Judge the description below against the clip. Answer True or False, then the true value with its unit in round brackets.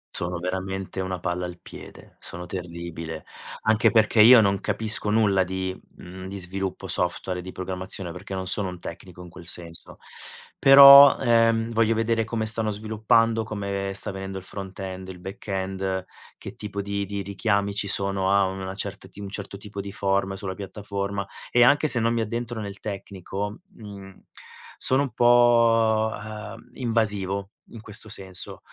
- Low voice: True (100 Hz)